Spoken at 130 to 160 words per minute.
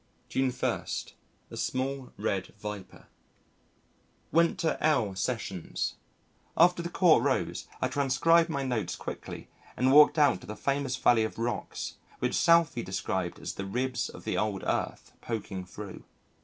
Yes: average, 145 wpm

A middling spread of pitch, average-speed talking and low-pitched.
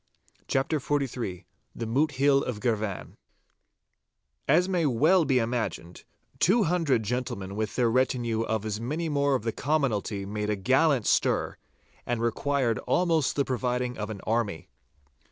Yes: average, 4.6 semitones; average, 145 wpm; low, 125 Hz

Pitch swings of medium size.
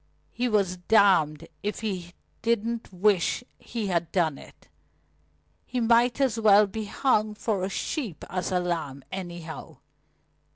Yes: average, 4.3 semitones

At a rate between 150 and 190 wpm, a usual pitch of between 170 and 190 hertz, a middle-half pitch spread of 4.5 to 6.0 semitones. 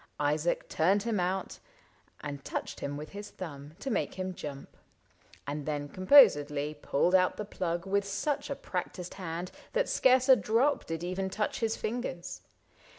Yes: average, 160 wpm; medium, 185 Hz; wide, 5.5 semitones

